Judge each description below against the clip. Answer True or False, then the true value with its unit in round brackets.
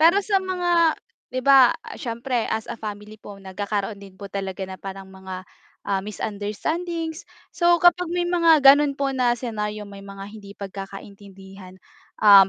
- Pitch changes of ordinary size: False (8.1 semitones)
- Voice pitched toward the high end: True (215 Hz)